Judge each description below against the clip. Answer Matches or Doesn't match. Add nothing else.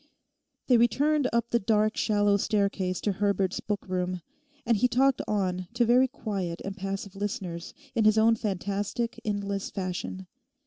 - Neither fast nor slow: Matches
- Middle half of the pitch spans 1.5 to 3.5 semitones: Matches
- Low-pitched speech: Doesn't match